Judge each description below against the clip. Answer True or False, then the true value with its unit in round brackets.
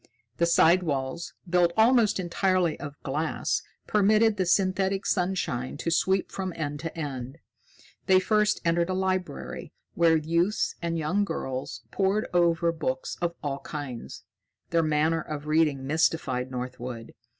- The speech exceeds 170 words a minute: False (140 wpm)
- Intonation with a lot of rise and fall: False (4.2 semitones)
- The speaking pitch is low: False (170 Hz)